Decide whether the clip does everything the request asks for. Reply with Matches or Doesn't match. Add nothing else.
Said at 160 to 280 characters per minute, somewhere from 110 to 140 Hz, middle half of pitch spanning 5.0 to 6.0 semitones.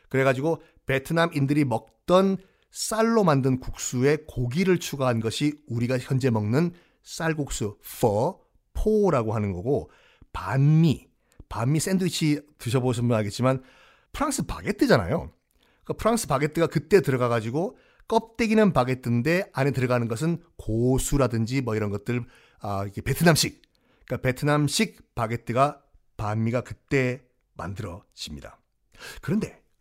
Doesn't match